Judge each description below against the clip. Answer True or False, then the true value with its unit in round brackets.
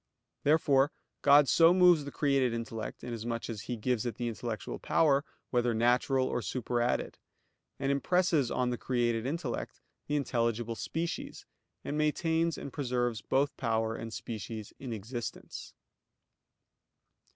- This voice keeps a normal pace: False (130 wpm)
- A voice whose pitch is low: True (125 Hz)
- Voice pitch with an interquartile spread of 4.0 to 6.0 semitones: False (3.6 semitones)